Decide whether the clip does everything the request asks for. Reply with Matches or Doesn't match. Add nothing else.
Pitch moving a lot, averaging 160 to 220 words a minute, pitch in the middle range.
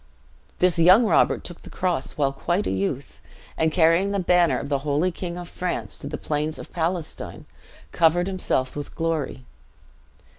Doesn't match